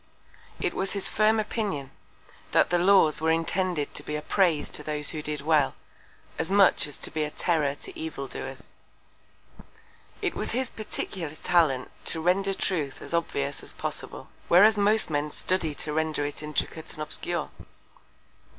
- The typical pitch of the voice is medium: Yes, medium, 160 Hz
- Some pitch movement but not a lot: Yes, average, 4.4 semitones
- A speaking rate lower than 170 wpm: Yes, average, 160 wpm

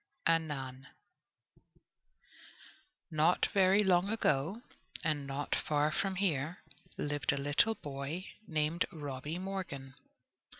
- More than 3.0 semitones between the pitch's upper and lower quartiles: Yes, average, 4.7 semitones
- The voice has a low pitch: No, medium, 155 Hz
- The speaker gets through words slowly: Yes, slow, 95 wpm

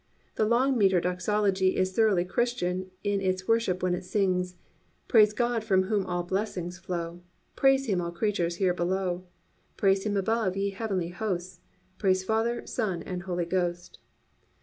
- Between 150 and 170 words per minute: Yes, average, 155 wpm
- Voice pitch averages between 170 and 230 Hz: Yes, high, 190 Hz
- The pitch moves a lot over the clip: No, average, 2.9 semitones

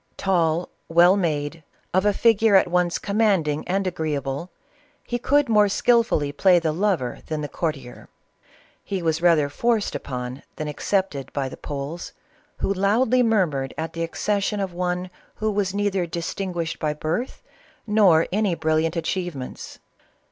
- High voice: No, medium, 175 Hz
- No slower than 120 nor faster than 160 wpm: Yes, average, 150 wpm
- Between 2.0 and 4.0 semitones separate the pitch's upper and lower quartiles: No, average, 4.4 semitones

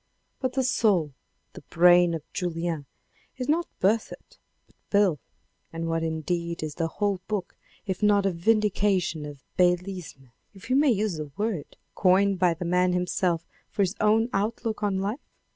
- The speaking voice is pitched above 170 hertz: Yes, medium, 185 Hz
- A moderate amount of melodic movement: Yes, average, 3.8 semitones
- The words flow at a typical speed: Yes, average, 160 wpm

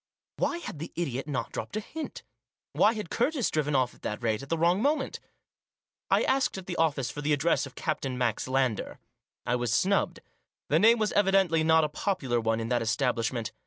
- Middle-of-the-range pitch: Yes, medium, 150 Hz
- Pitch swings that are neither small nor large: No, wide, 7.6 semitones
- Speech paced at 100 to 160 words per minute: No, average, 200 wpm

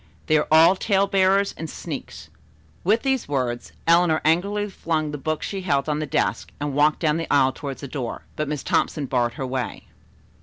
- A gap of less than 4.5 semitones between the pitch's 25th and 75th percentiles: No, average, 4.8 semitones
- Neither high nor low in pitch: Yes, medium, 155 Hz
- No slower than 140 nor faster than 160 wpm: No, average, 195 wpm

